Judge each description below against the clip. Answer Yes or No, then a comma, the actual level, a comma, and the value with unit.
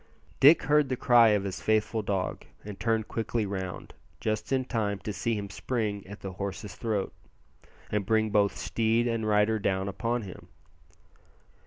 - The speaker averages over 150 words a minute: Yes, average, 165 wpm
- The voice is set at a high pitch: No, low, 105 Hz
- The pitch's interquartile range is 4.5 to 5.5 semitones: No, narrow, 2.4 semitones